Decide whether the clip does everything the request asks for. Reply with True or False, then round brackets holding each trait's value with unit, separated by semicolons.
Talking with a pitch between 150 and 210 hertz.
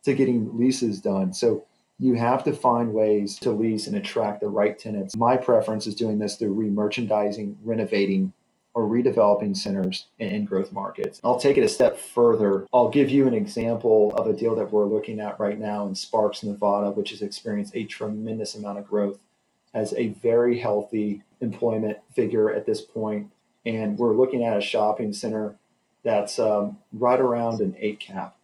False (110 Hz)